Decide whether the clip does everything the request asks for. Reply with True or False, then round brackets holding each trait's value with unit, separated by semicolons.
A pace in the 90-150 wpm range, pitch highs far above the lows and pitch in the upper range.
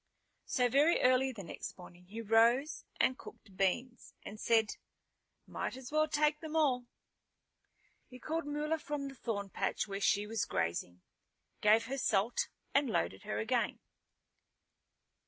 True (145 wpm; 5.9 semitones; 240 Hz)